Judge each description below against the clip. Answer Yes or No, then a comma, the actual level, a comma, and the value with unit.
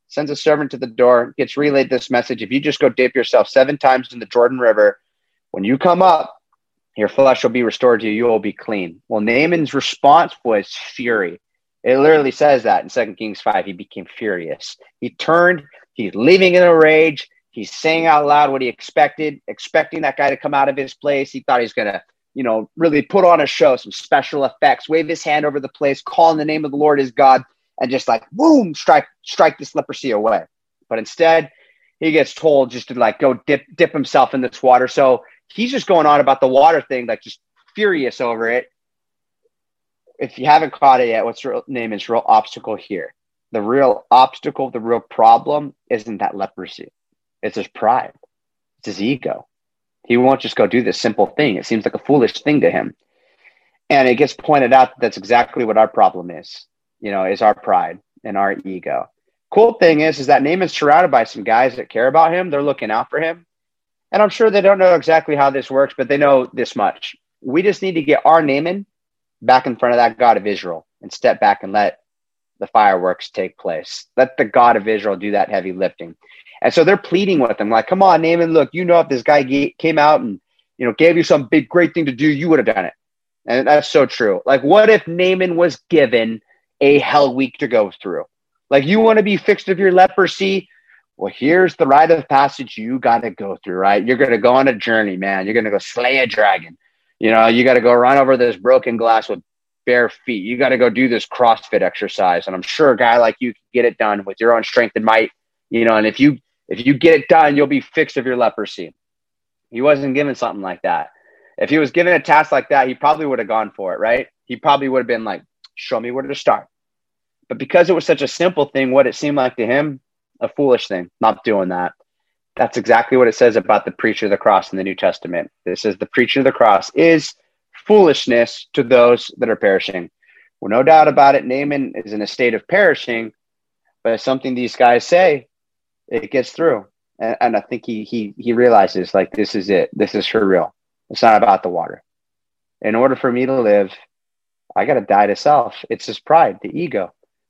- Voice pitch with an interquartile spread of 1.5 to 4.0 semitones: No, average, 5.0 semitones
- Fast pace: Yes, fast, 225 wpm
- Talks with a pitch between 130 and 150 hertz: Yes, low, 135 Hz